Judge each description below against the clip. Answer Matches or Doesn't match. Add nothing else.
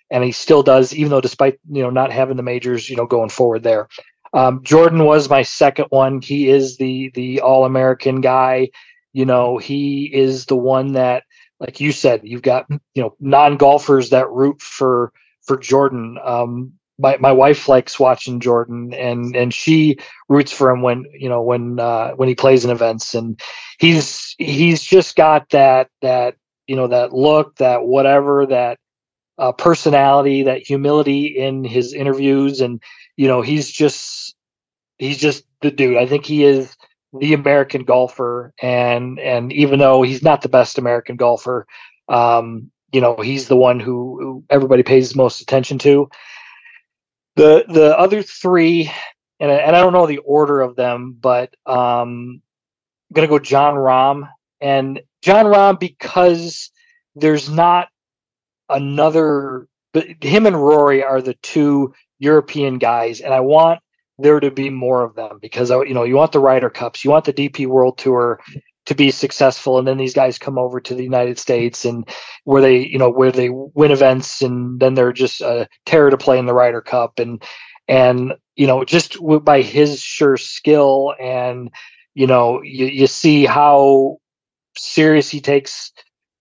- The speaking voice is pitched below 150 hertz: Matches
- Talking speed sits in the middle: Matches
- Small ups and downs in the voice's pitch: Matches